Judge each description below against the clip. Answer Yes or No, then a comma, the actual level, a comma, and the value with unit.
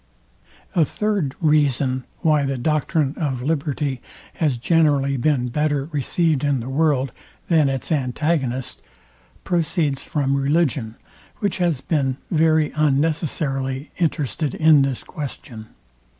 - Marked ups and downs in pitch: No, average, 2.9 semitones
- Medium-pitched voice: Yes, medium, 145 Hz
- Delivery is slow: Yes, slow, 115 wpm